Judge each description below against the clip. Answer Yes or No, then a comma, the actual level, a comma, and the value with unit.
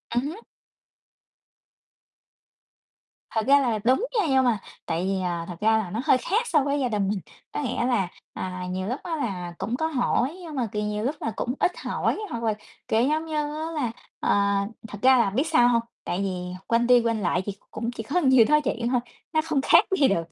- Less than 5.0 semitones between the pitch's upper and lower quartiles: No, average, 5.3 semitones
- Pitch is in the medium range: No, high, 240 Hz